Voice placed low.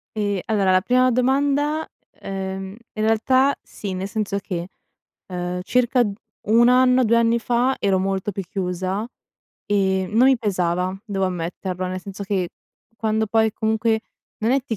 No: high, 215 Hz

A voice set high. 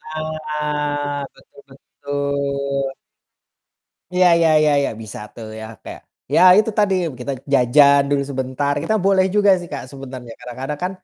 No: medium, 140 Hz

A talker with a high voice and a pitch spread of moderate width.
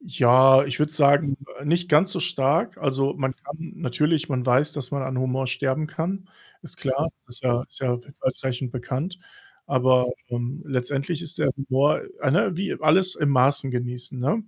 No: low, 135 Hz; average, 3.3 semitones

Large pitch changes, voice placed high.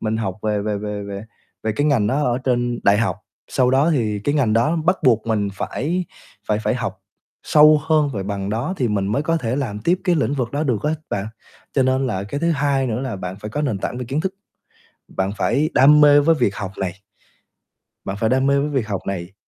No: wide, 5.7 semitones; low, 125 Hz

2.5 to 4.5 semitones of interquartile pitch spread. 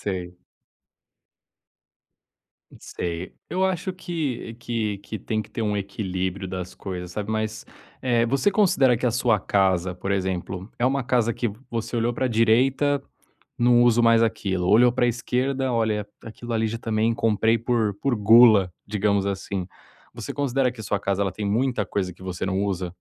Yes: average, 3.7 semitones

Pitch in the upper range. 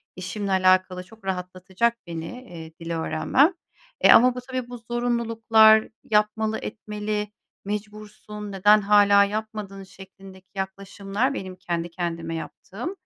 Yes: high, 205 Hz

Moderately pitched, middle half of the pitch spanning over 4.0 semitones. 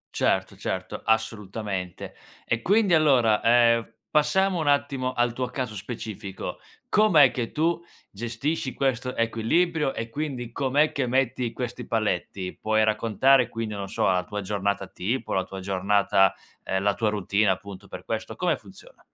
No: low, 115 Hz; average, 4.7 semitones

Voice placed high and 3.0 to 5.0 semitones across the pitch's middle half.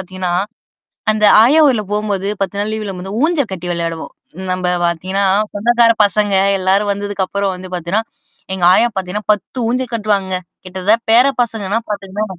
No: high, 200 Hz; narrow, 2.4 semitones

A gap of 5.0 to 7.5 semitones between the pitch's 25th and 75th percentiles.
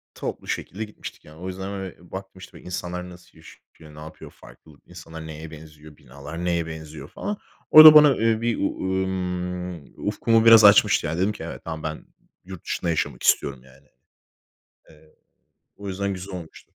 No: average, 3.8 semitones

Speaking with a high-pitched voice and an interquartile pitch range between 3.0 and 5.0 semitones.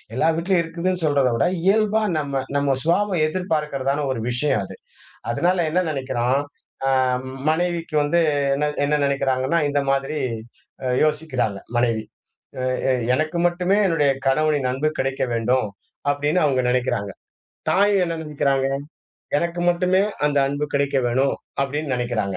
No: medium, 145 Hz; average, 4.2 semitones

